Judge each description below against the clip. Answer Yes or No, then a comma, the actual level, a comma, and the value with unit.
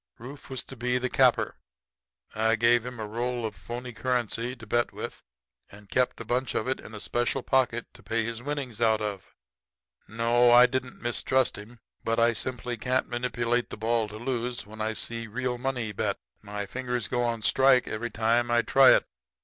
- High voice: No, low, 120 Hz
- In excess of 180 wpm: Yes, average, 200 wpm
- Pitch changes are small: Yes, narrow, 1.9 semitones